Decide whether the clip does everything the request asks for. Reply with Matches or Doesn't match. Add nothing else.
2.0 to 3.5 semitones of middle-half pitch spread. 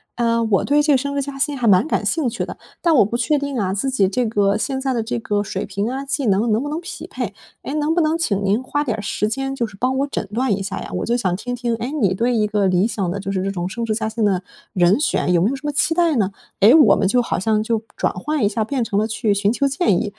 Doesn't match